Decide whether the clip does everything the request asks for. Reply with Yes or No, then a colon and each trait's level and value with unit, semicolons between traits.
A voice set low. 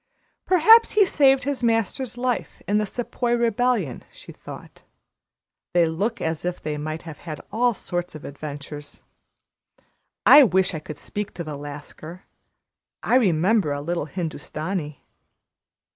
No: medium, 180 Hz